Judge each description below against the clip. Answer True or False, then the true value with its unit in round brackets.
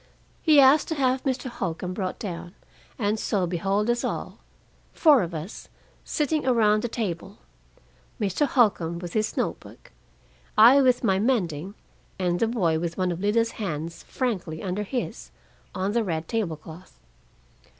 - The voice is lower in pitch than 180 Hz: False (205 Hz)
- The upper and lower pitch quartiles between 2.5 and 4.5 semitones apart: False (5.5 semitones)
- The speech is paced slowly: False (155 wpm)